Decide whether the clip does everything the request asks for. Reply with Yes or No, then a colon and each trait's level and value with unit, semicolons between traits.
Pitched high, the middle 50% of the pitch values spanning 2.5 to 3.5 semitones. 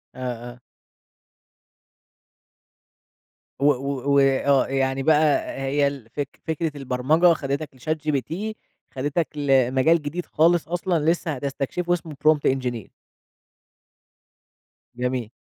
No: medium, 140 Hz; average, 3.1 semitones